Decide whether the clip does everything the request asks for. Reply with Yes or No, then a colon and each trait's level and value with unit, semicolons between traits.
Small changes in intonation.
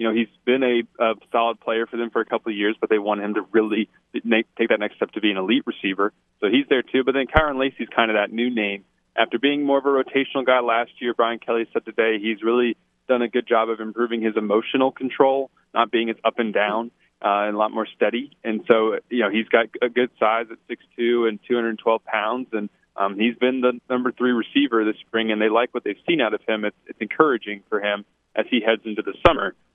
Yes: narrow, 2.1 semitones